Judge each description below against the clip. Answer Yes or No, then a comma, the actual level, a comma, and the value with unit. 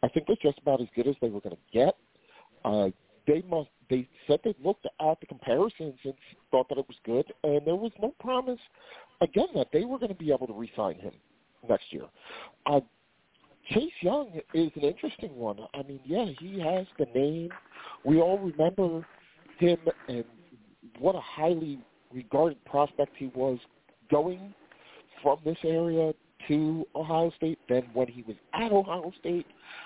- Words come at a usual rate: Yes, average, 175 wpm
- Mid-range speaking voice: Yes, medium, 155 Hz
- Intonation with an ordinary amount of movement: Yes, average, 4.4 semitones